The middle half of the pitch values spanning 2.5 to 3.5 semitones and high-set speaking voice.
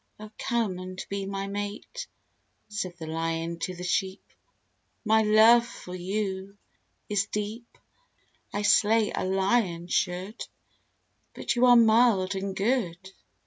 Yes: average, 2.9 semitones; high, 200 Hz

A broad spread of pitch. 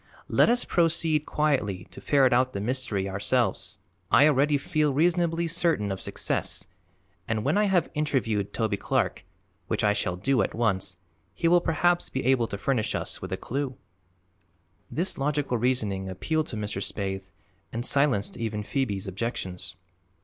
Yes: wide, 6.8 semitones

